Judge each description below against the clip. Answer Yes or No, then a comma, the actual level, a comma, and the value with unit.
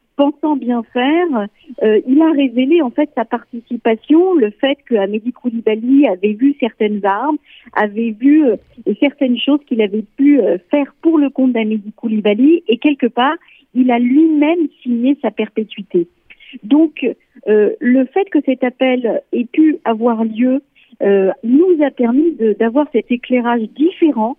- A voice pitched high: Yes, very high, 255 Hz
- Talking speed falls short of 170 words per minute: Yes, average, 150 wpm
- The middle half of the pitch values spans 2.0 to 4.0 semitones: No, average, 4.5 semitones